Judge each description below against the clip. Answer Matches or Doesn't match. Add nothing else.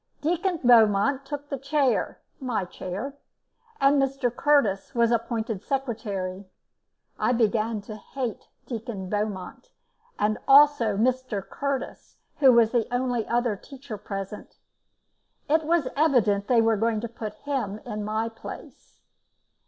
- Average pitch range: Matches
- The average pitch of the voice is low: Doesn't match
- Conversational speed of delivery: Doesn't match